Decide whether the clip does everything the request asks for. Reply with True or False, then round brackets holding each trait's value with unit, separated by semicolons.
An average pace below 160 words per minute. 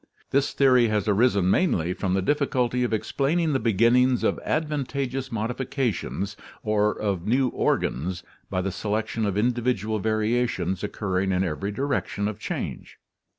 True (140 wpm)